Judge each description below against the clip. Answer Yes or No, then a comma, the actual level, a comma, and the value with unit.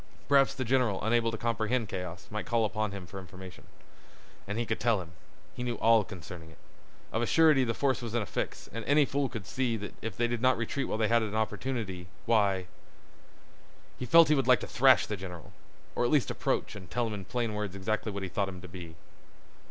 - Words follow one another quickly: Yes, fast, 225 wpm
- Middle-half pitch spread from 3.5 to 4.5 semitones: Yes, average, 4.0 semitones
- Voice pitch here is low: Yes, low, 110 Hz